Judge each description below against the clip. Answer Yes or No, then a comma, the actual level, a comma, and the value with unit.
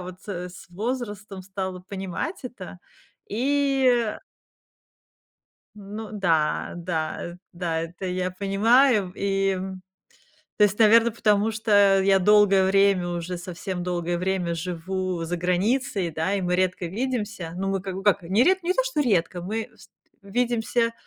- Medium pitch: No, high, 195 Hz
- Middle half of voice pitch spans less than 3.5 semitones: Yes, average, 3.1 semitones